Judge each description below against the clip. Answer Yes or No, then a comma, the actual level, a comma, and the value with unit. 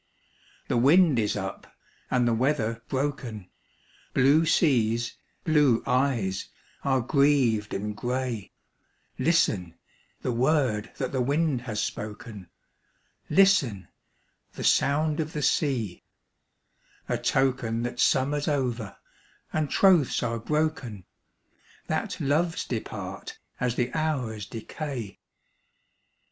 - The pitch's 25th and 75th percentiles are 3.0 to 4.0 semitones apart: No, average, 4.6 semitones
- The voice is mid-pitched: No, low, 130 Hz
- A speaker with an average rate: No, slow, 105 wpm